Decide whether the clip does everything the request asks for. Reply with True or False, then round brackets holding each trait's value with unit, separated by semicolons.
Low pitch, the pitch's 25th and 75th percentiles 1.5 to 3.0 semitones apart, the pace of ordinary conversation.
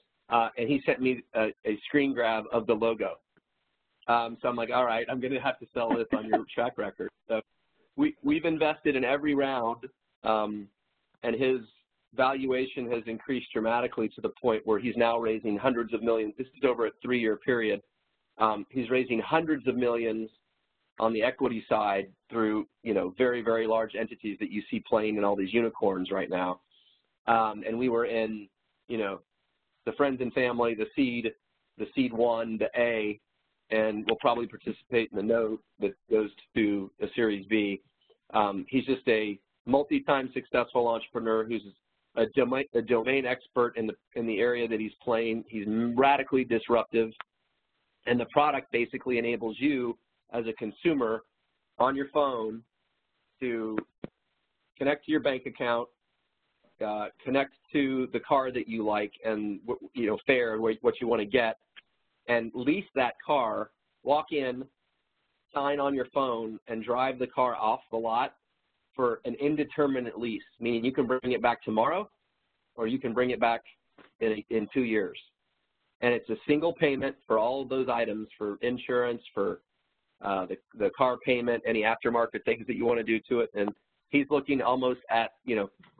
True (115 Hz; 2.7 semitones; 175 wpm)